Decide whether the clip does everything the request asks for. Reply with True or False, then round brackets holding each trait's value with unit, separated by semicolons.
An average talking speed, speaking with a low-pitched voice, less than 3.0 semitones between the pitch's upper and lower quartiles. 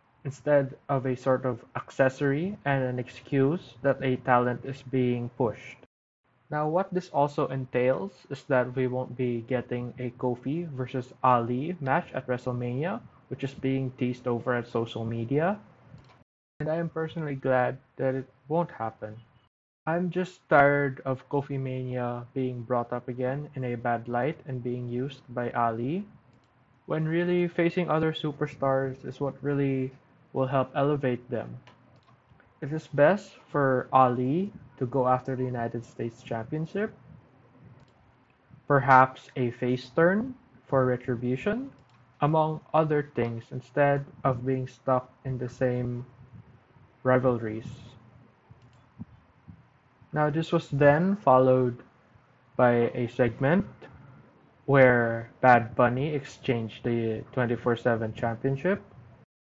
False (125 wpm; 130 Hz; 2.4 semitones)